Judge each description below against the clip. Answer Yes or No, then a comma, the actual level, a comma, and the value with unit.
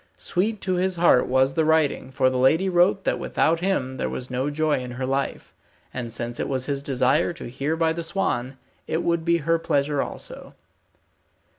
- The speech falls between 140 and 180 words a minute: No, average, 195 wpm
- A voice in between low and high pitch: Yes, medium, 145 Hz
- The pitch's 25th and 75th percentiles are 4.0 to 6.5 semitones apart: Yes, average, 4.6 semitones